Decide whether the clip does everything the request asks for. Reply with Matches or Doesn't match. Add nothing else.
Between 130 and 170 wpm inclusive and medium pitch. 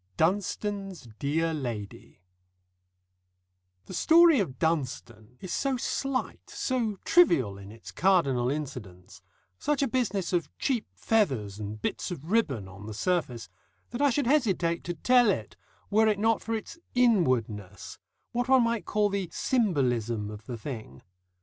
Matches